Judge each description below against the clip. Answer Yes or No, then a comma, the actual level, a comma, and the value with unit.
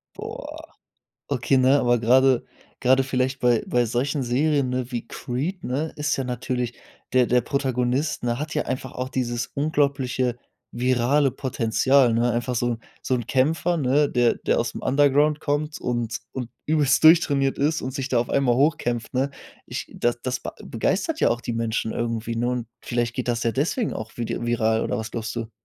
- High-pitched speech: No, low, 125 Hz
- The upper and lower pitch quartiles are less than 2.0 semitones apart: No, average, 2.7 semitones